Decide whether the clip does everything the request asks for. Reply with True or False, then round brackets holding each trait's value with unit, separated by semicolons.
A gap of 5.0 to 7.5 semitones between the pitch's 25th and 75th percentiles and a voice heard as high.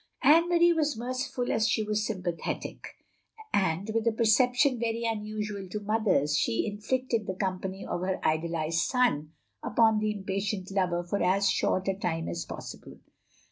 False (3.9 semitones; 210 Hz)